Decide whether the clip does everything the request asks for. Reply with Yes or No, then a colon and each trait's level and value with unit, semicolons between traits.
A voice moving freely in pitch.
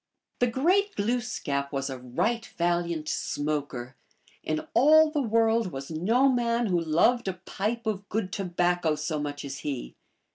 Yes: wide, 7.6 semitones